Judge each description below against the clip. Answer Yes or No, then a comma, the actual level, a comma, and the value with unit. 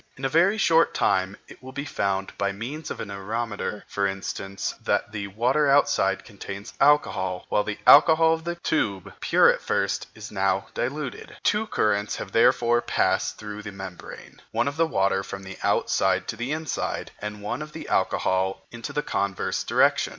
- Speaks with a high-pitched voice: No, low, 105 Hz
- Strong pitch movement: Yes, wide, 6.4 semitones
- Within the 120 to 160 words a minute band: No, average, 175 wpm